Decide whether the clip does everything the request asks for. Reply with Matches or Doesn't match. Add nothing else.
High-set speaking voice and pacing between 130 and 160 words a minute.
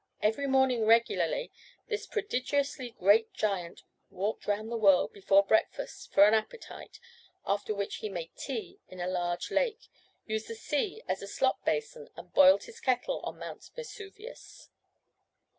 Matches